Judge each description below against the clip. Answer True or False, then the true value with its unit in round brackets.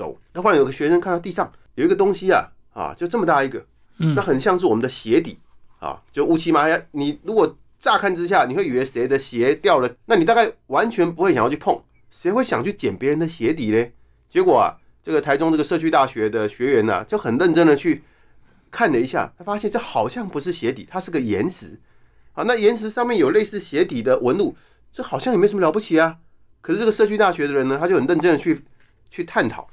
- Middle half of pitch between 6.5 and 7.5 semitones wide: True (7.1 semitones)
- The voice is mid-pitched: True (175 Hz)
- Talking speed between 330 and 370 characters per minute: True (340 characters per minute)